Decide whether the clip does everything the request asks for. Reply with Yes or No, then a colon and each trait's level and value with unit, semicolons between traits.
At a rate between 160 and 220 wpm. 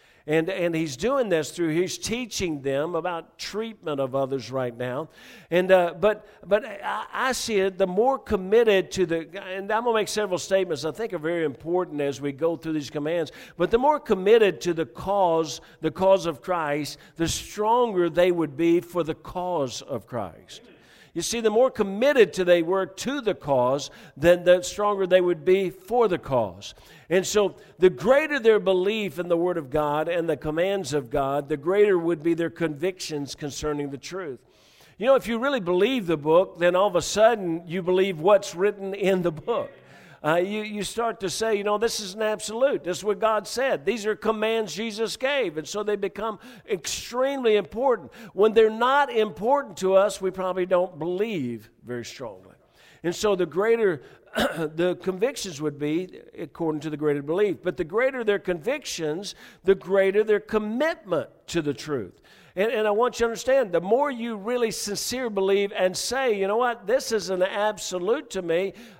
Yes: average, 190 wpm